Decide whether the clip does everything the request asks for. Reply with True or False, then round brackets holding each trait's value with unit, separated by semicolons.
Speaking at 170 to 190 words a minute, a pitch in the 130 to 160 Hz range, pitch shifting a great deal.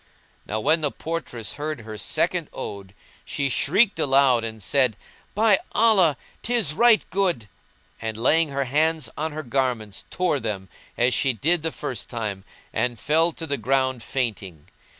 False (150 wpm; 135 Hz; 6.1 semitones)